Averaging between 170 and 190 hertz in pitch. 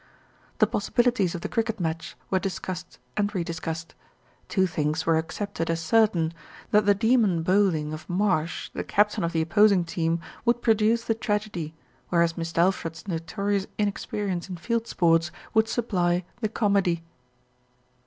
Yes: medium, 185 Hz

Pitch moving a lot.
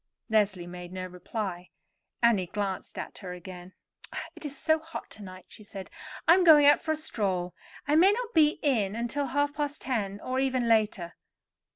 Yes: wide, 7.6 semitones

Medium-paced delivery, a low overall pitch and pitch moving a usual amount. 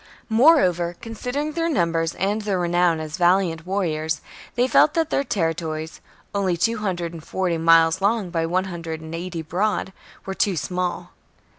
No: average, 170 wpm; medium, 180 Hz; average, 3.9 semitones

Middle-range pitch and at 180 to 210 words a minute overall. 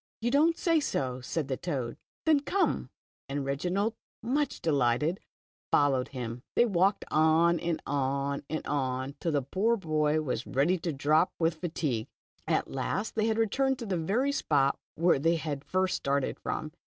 No: medium, 160 Hz; average, 165 wpm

